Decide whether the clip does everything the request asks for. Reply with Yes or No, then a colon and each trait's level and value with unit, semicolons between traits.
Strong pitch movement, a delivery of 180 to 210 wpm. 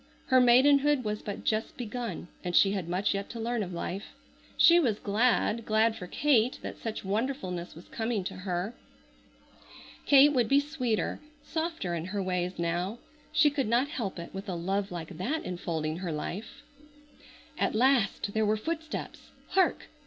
No: wide, 5.7 semitones; average, 165 wpm